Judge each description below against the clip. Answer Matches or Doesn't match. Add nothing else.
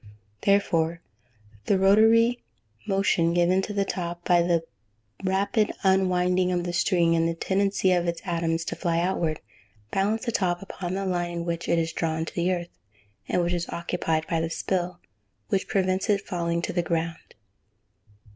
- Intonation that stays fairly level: Matches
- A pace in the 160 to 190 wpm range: Matches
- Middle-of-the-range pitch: Matches